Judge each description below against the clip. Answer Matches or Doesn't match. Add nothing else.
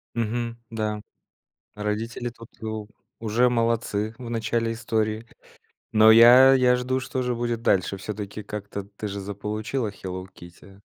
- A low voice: Matches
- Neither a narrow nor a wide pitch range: Doesn't match